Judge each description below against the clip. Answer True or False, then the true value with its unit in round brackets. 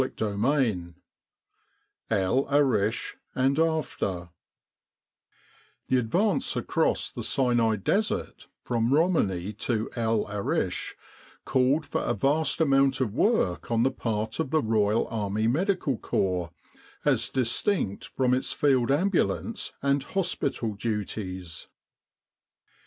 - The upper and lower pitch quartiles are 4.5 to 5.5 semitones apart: True (5.2 semitones)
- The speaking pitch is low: True (120 Hz)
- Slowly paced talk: True (110 wpm)